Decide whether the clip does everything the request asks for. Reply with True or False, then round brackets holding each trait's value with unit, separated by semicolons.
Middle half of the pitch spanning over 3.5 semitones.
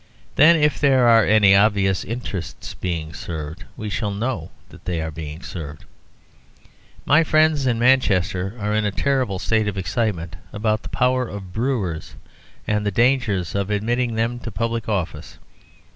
True (4.7 semitones)